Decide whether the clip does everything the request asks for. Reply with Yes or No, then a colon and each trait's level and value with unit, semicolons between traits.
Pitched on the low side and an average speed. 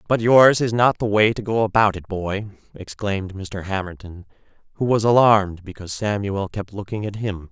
Yes: low, 105 Hz; average, 175 wpm